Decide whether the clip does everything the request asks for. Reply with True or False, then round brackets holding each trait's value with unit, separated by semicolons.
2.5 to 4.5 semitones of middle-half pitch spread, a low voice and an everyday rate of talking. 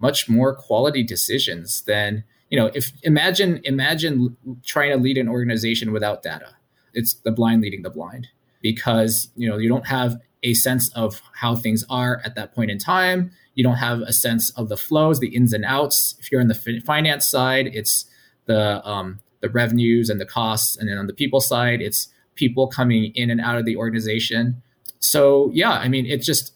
True (2.8 semitones; 120 Hz; 195 wpm)